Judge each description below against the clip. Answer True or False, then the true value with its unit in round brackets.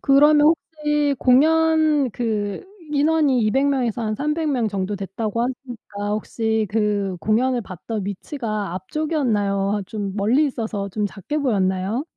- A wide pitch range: True (5.9 semitones)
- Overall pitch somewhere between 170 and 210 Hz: False (230 Hz)